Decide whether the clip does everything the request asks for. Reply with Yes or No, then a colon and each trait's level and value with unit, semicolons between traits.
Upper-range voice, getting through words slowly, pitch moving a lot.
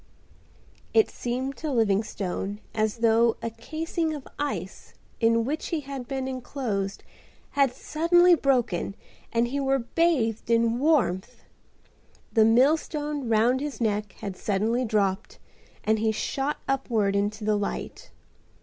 No: high, 235 Hz; slow, 130 wpm; average, 4.3 semitones